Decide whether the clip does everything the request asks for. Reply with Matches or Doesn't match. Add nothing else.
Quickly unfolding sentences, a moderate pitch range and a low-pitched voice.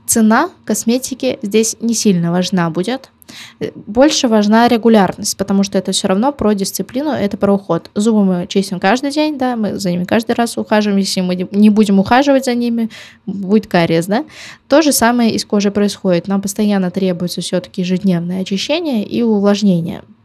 Doesn't match